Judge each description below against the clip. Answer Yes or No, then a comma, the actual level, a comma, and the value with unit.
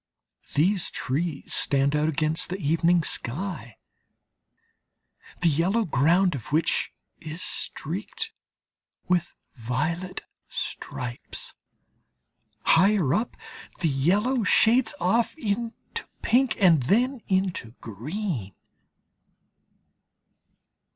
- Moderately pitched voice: Yes, medium, 170 Hz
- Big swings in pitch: Yes, wide, 5.9 semitones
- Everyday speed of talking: No, slow, 85 wpm